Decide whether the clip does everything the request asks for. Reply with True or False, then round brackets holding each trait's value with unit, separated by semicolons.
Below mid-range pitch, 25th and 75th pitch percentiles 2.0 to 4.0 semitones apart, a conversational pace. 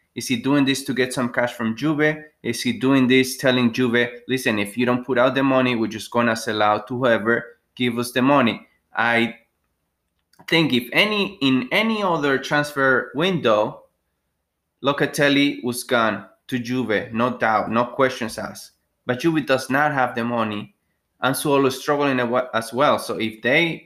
True (125 Hz; 2.7 semitones; 180 wpm)